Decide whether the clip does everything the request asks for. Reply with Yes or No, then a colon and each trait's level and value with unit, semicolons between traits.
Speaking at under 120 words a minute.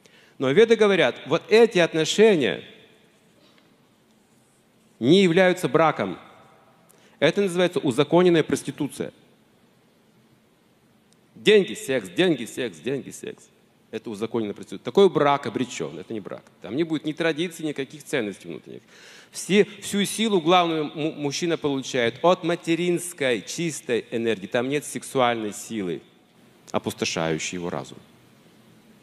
Yes: slow, 110 wpm